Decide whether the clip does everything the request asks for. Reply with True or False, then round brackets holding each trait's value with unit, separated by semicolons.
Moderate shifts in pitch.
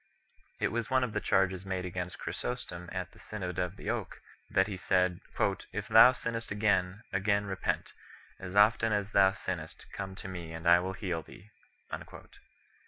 False (2.2 semitones)